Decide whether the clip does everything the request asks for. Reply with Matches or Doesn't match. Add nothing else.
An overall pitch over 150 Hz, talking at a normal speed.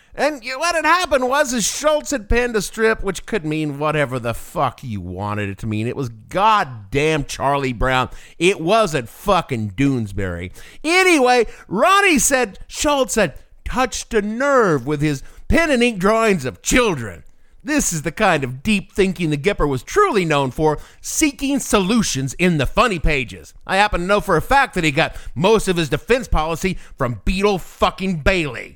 Matches